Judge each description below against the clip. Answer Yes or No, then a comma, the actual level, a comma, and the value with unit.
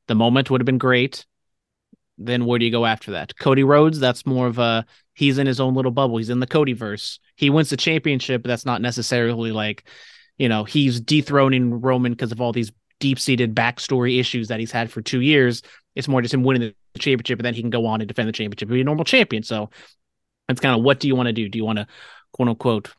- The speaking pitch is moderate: No, low, 125 Hz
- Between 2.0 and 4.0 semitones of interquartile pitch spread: Yes, narrow, 2.5 semitones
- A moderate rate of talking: No, fast, 250 wpm